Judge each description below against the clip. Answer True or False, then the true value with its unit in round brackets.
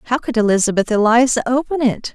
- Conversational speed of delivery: True (170 wpm)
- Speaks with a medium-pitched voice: False (235 Hz)